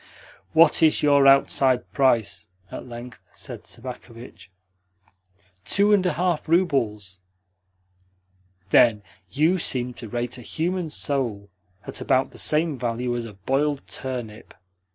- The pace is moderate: No, slow, 125 wpm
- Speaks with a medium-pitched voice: No, low, 130 Hz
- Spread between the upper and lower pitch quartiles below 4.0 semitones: No, average, 4.6 semitones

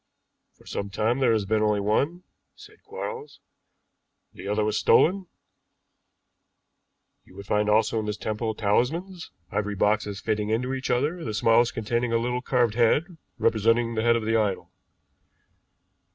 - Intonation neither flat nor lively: Yes, average, 3.2 semitones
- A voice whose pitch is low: Yes, low, 115 Hz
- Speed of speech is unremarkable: Yes, average, 150 wpm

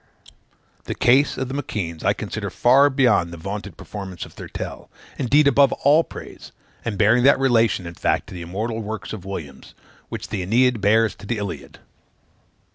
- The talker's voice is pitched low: Yes, low, 110 Hz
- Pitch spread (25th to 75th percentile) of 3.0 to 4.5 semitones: No, average, 5.1 semitones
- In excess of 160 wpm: Yes, average, 175 wpm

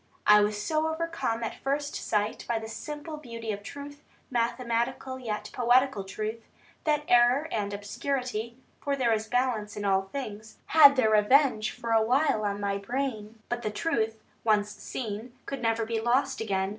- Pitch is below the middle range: No, high, 230 Hz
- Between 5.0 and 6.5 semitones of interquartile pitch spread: No, average, 3.9 semitones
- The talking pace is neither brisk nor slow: Yes, average, 170 wpm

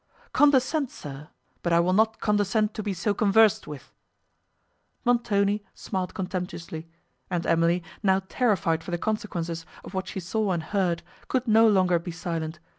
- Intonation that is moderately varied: Yes, average, 4.0 semitones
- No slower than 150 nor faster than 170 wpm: Yes, average, 155 wpm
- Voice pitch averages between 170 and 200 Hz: Yes, high, 190 Hz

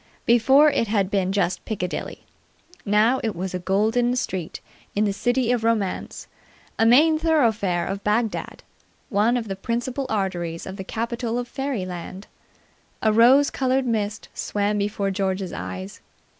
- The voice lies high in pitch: Yes, high, 215 Hz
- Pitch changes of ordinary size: Yes, average, 3.9 semitones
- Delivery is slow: No, average, 145 wpm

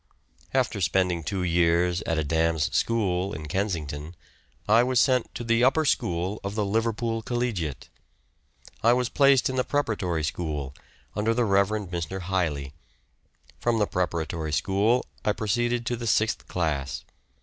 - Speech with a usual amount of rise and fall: No, wide, 5.7 semitones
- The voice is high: No, low, 100 Hz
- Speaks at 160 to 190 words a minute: No, average, 150 wpm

